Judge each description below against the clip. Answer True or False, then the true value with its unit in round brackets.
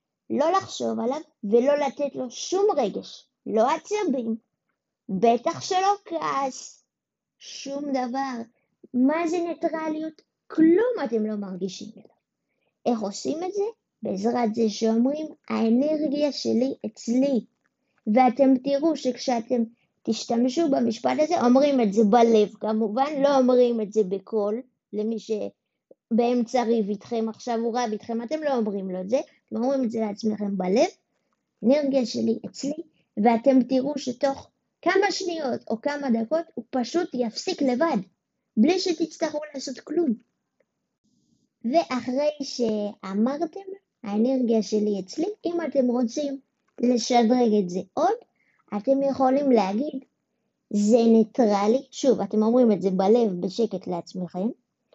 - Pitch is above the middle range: True (250 Hz)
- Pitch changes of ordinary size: True (4.4 semitones)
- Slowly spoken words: False (125 wpm)